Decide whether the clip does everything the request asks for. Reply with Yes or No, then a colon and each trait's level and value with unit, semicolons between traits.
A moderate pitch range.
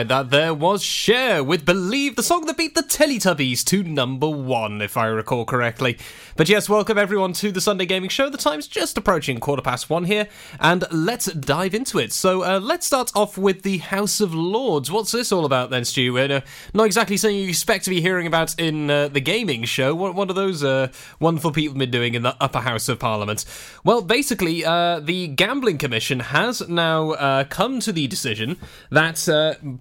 No: wide, 6.8 semitones